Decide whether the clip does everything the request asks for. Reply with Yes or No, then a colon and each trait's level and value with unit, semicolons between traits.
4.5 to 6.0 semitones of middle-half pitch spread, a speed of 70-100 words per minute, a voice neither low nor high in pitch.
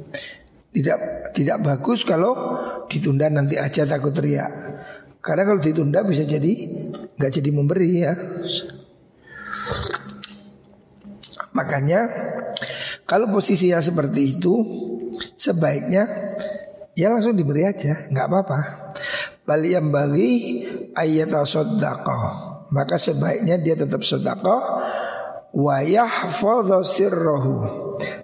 Yes: average, 5.0 semitones; slow, 85 wpm; medium, 165 Hz